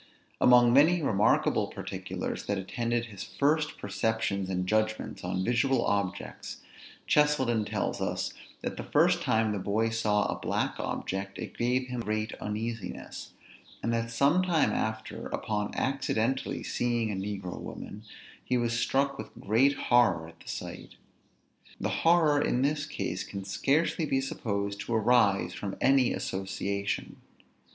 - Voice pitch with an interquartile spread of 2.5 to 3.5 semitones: No, average, 4.7 semitones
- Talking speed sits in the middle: Yes, average, 145 wpm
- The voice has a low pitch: Yes, low, 115 Hz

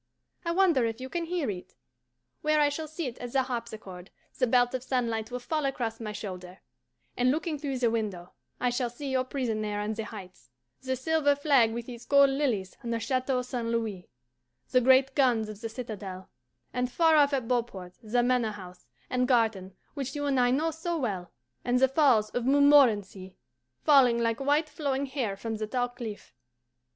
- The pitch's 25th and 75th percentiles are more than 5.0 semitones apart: No, average, 3.9 semitones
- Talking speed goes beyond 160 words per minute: Yes, average, 190 wpm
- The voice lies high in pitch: Yes, high, 245 Hz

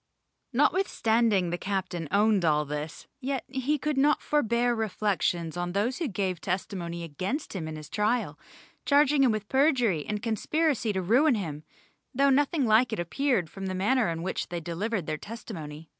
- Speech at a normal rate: Yes, average, 170 wpm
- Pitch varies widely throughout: Yes, wide, 6.9 semitones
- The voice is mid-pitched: No, high, 210 Hz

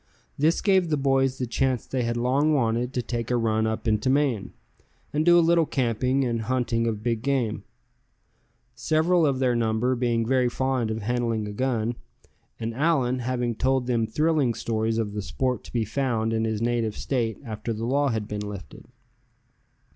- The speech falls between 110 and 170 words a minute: No, average, 185 wpm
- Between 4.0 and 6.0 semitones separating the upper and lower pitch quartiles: No, average, 2.9 semitones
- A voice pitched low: Yes, low, 120 Hz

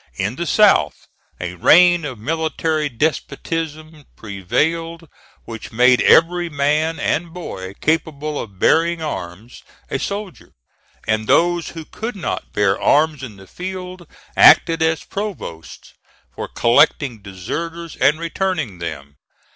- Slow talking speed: Yes, slow, 125 wpm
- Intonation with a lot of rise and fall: Yes, wide, 7.0 semitones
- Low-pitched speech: No, medium, 155 Hz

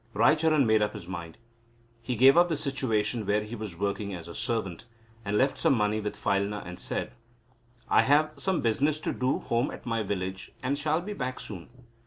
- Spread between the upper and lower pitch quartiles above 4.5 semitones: Yes, average, 5.2 semitones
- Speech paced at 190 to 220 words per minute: Yes, fast, 205 wpm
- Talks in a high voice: No, low, 115 Hz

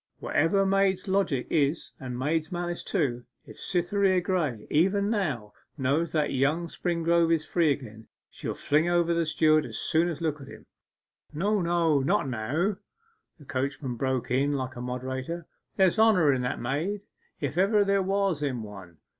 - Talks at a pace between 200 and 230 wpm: No, average, 165 wpm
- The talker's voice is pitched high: No, medium, 160 Hz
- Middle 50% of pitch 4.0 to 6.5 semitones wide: Yes, average, 5.2 semitones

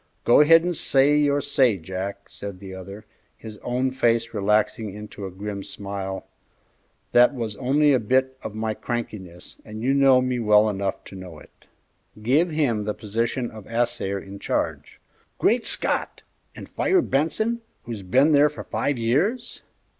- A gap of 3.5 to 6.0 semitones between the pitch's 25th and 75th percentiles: Yes, average, 5.3 semitones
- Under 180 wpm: Yes, average, 160 wpm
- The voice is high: No, low, 115 Hz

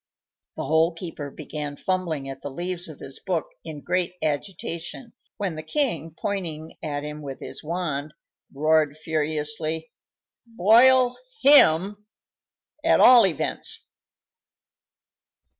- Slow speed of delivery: Yes, slow, 115 wpm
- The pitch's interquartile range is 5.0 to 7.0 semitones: No, average, 3.6 semitones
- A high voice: No, medium, 160 Hz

